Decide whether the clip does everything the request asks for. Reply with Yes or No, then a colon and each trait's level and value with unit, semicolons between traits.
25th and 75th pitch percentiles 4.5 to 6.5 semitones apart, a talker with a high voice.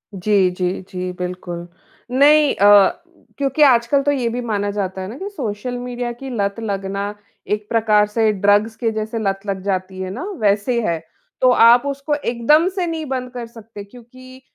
No: average, 4.1 semitones; high, 225 Hz